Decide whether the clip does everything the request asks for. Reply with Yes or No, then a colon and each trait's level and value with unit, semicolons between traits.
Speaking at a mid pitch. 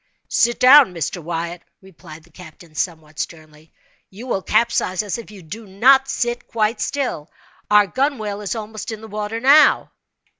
No: high, 210 Hz